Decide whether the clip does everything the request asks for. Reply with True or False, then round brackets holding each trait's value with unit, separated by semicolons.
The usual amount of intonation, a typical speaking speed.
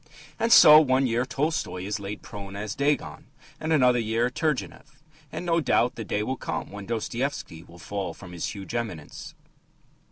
False (5.7 semitones; 170 wpm)